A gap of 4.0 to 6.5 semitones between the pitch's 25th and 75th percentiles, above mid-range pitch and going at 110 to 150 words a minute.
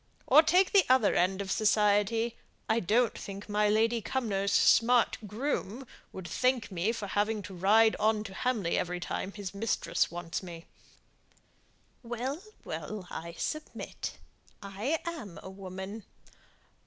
No: average, 3.5 semitones; high, 210 Hz; average, 140 wpm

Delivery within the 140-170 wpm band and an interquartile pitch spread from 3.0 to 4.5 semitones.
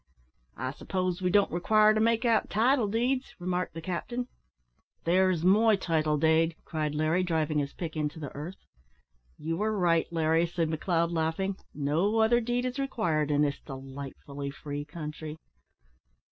No: average, 155 wpm; average, 5.3 semitones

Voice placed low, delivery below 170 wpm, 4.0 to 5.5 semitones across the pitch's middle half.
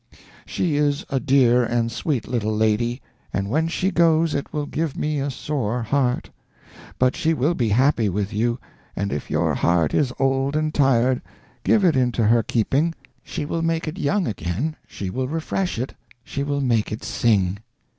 No: low, 130 Hz; average, 180 wpm; average, 4.8 semitones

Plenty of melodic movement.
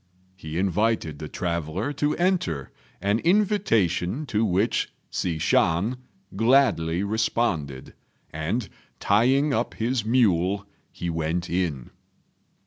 Yes: wide, 6.1 semitones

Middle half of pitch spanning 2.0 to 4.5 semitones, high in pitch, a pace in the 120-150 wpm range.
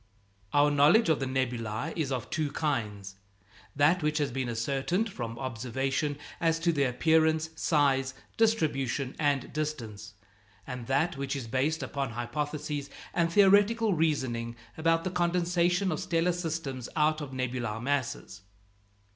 No: average, 4.2 semitones; medium, 145 Hz; average, 140 wpm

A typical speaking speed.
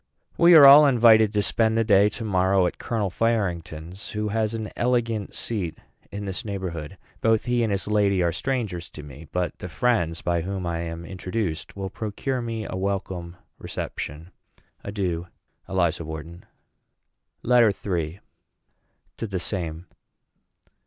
Yes: average, 150 wpm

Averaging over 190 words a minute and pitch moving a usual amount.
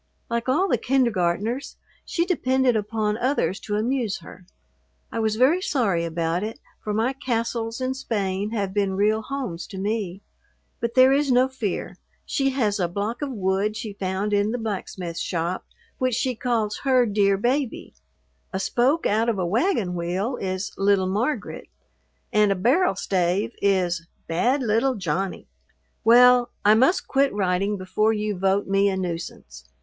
No: average, 160 wpm; average, 4.5 semitones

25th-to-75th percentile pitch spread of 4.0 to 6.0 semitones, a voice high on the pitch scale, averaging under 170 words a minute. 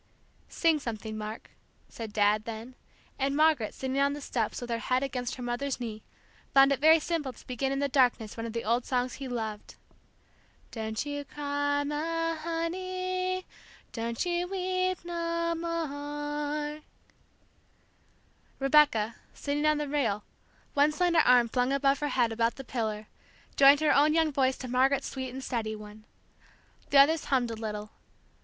Yes: average, 4.5 semitones; very high, 275 Hz; average, 160 wpm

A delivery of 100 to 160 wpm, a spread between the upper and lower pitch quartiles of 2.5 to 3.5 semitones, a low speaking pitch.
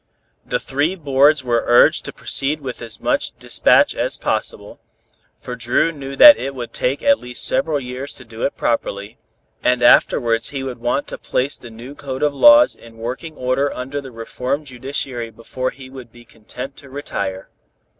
No: average, 180 wpm; average, 2.8 semitones; low, 130 Hz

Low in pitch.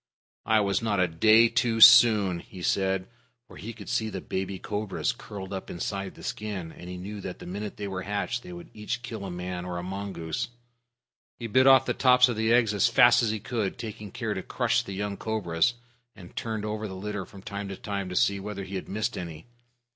Yes: low, 100 Hz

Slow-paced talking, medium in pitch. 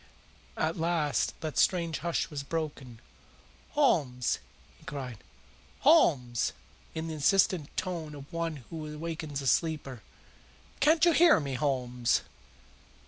Yes: slow, 120 wpm; medium, 155 Hz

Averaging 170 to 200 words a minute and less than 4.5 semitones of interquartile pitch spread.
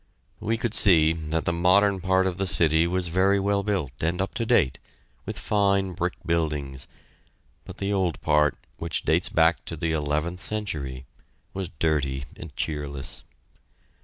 No: average, 160 wpm; average, 4.0 semitones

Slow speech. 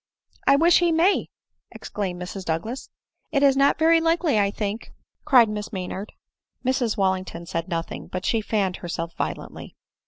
No: average, 175 wpm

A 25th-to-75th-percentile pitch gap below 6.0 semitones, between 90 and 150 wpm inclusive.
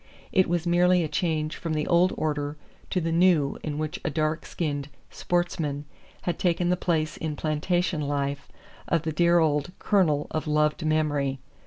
No: narrow, 2.6 semitones; average, 170 wpm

